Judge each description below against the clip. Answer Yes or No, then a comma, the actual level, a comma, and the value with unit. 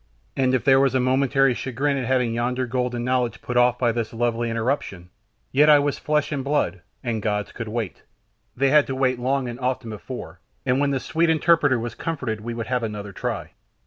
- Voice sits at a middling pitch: No, low, 125 Hz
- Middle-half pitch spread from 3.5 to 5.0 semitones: No, average, 2.7 semitones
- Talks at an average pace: No, fast, 210 wpm